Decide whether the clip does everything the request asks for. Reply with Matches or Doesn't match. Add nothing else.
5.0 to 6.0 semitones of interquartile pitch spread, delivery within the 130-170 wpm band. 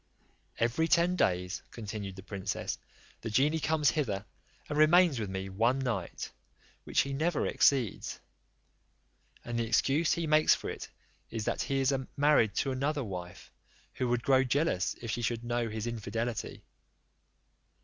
Matches